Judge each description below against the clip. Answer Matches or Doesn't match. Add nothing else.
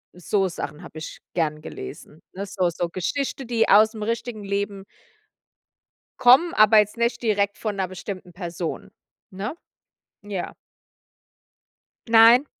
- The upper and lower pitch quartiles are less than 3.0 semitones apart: Doesn't match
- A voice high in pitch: Matches